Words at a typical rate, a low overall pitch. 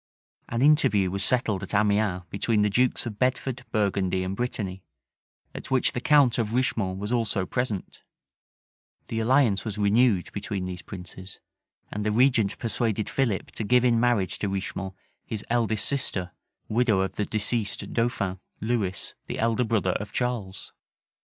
Yes: average, 155 wpm; low, 110 Hz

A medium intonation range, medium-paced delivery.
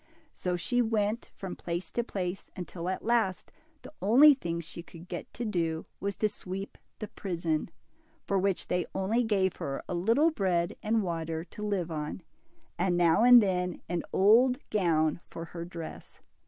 Yes: average, 3.9 semitones; average, 180 wpm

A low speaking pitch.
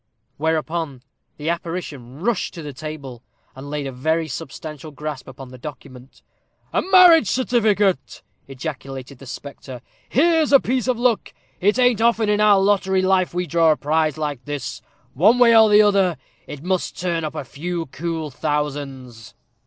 No: medium, 160 Hz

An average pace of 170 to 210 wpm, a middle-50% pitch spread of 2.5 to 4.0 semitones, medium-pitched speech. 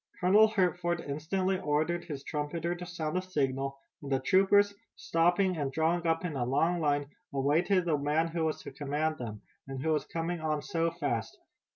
Yes: average, 185 wpm; average, 3.4 semitones; medium, 160 Hz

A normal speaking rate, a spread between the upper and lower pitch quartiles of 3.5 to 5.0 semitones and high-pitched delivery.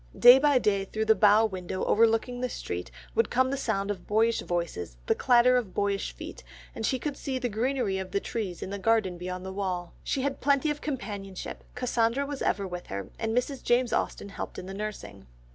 No: fast, 210 wpm; average, 4.6 semitones; high, 220 Hz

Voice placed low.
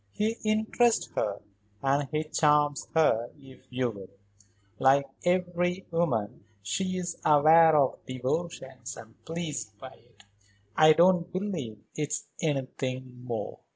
No: medium, 150 Hz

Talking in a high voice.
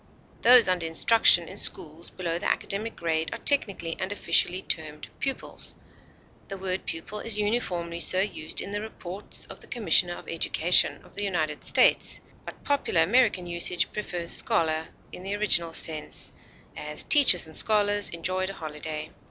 No: medium, 180 Hz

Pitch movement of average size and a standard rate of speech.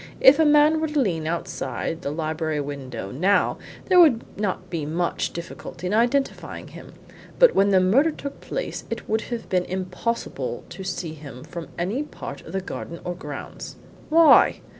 No: wide, 8.4 semitones; average, 175 wpm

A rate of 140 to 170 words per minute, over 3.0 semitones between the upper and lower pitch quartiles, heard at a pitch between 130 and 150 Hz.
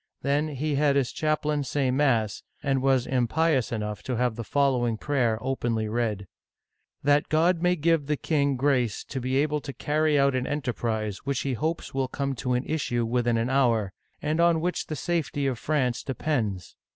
No: average, 190 wpm; average, 3.7 semitones; low, 135 Hz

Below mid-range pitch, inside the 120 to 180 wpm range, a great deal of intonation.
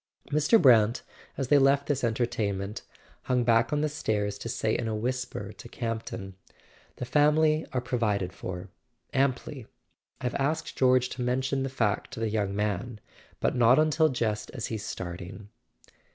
No: low, 120 Hz; average, 155 wpm; average, 4.1 semitones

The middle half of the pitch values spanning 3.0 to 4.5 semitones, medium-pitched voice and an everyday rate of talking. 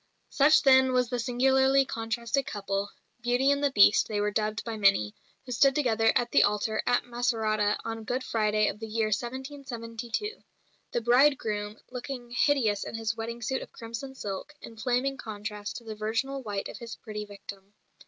No: average, 3.5 semitones; high, 230 Hz; average, 175 wpm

